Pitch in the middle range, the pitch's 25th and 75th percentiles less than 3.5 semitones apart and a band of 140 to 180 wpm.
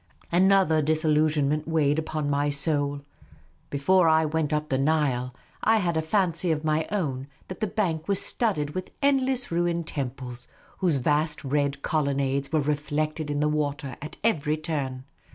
Yes: medium, 155 Hz; average, 2.7 semitones; average, 160 wpm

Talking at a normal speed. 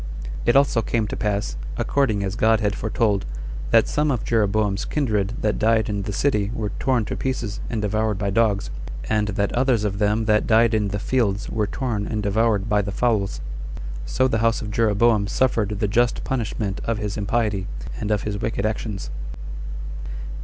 Yes: average, 180 wpm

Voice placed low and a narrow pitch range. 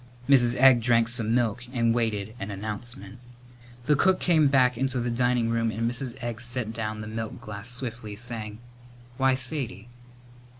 Yes: low, 120 Hz; narrow, 2.2 semitones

